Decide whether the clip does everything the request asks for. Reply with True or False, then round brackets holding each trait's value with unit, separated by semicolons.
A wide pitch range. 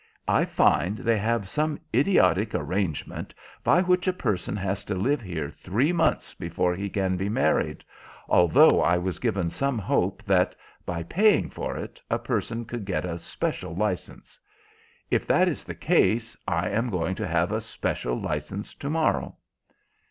False (4.8 semitones)